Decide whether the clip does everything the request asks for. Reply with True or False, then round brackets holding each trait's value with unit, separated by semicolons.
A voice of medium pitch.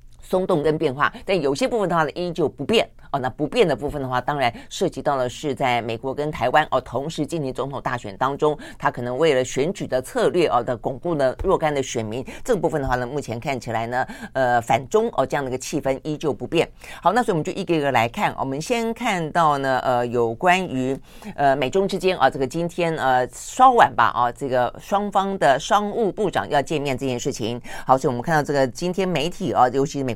True (145 Hz)